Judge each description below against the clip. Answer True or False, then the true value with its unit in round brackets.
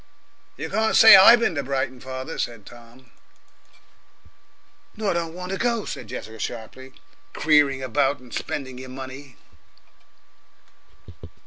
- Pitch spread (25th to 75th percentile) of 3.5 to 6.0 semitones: True (4.6 semitones)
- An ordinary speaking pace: False (125 wpm)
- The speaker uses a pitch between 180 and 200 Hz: False (135 Hz)